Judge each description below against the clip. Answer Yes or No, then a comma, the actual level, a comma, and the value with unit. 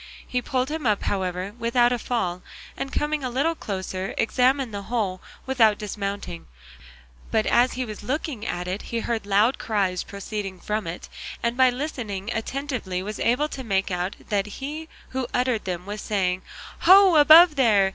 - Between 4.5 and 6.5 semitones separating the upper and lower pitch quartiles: Yes, average, 4.9 semitones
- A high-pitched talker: Yes, high, 225 Hz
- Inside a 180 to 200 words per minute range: No, average, 170 wpm